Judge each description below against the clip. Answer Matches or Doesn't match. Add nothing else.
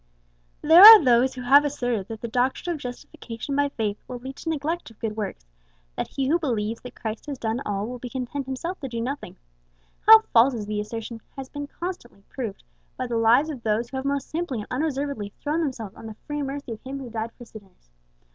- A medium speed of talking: Doesn't match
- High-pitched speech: Matches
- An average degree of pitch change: Matches